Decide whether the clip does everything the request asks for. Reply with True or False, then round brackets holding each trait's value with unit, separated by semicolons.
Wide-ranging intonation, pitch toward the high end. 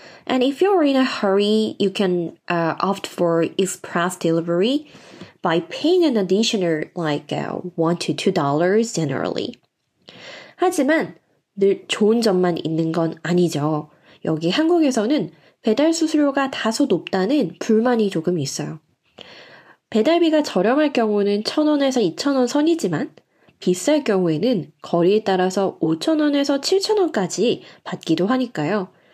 True (8.2 semitones; 200 Hz)